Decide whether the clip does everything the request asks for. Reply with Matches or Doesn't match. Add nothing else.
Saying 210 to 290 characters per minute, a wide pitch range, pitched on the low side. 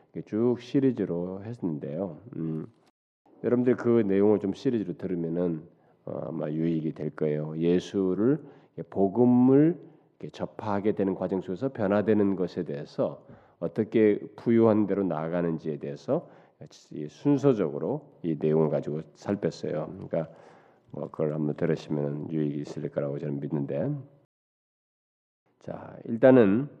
Matches